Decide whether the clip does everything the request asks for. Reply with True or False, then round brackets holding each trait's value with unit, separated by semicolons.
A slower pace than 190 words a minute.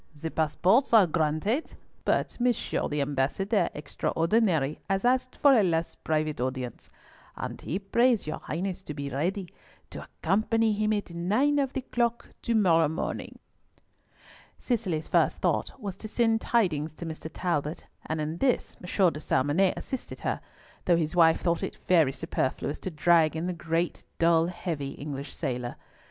True (160 wpm)